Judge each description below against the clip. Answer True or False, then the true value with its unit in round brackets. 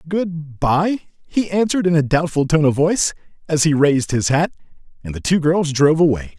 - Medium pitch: True (155 Hz)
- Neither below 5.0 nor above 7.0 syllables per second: True (5.5 syllables/s)